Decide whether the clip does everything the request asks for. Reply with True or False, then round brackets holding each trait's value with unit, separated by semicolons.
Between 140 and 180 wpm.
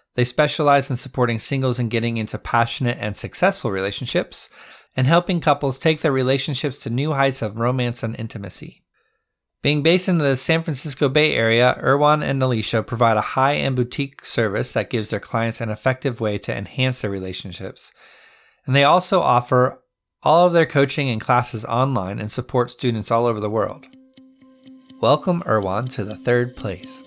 True (170 wpm)